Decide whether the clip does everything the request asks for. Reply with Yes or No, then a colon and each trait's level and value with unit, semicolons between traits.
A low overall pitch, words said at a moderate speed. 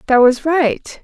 No: very high, 280 Hz; average, 175 wpm